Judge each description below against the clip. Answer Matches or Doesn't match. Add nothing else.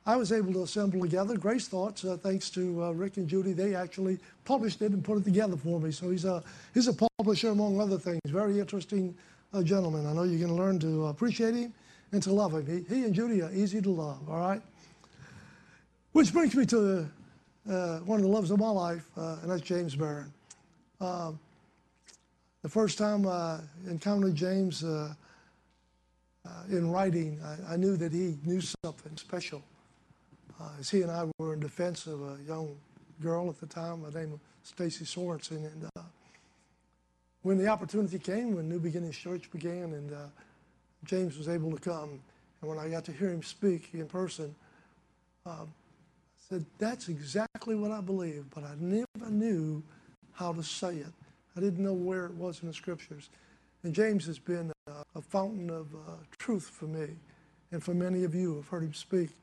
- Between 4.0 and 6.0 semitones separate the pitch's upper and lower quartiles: Doesn't match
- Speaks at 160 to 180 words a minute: Doesn't match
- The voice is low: Doesn't match